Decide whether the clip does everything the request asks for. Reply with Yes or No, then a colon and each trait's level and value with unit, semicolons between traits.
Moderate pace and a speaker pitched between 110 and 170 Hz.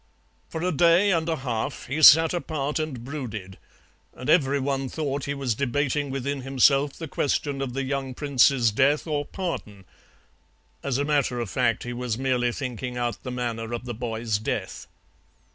Yes: average, 175 wpm; low, 135 Hz